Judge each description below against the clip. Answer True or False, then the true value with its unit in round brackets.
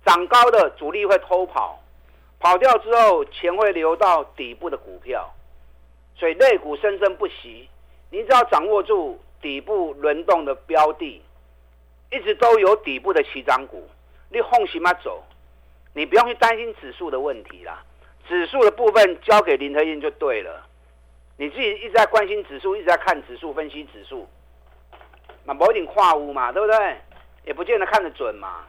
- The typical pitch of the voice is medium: True (180 Hz)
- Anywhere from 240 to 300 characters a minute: True (250 characters per minute)